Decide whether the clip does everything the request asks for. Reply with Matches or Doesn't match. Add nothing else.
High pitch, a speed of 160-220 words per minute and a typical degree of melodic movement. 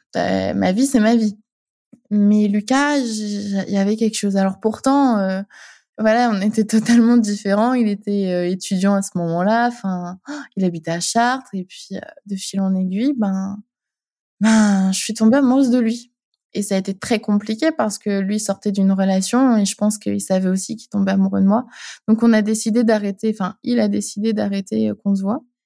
Matches